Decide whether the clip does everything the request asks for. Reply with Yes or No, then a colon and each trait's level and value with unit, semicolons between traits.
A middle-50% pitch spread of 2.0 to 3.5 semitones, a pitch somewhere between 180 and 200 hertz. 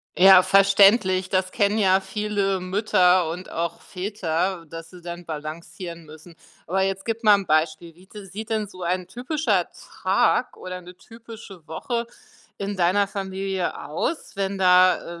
Yes: narrow, 2.5 semitones; medium, 185 Hz